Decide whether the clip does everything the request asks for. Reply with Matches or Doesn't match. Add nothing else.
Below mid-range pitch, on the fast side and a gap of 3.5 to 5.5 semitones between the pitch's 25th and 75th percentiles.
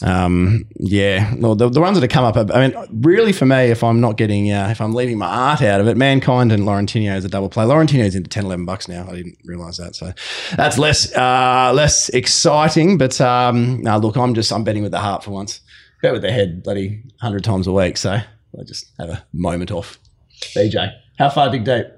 Matches